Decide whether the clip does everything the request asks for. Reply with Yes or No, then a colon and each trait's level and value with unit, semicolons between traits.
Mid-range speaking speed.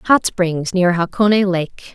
Yes: average, 155 wpm